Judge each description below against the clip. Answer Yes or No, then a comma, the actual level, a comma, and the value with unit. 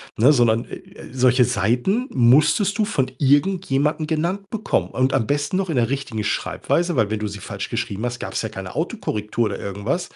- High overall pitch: No, low, 130 Hz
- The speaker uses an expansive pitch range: Yes, wide, 6.4 semitones